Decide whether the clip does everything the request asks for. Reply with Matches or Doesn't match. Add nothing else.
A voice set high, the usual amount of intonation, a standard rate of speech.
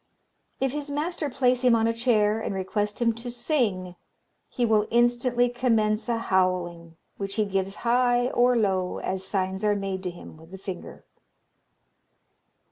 Matches